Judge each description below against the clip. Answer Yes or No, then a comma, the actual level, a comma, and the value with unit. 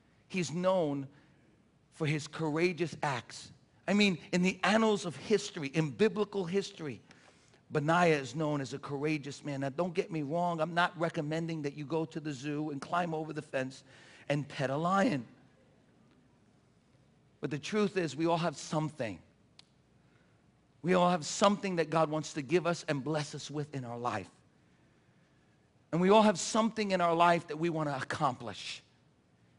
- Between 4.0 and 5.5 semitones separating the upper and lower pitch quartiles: No, average, 3.6 semitones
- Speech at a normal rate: Yes, average, 170 wpm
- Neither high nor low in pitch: Yes, medium, 155 Hz